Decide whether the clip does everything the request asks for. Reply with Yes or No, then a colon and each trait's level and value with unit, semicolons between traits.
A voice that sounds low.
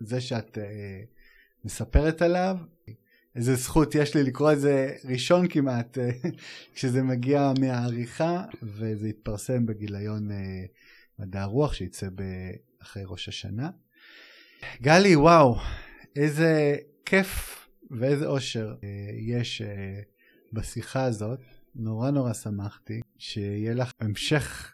Yes: low, 125 Hz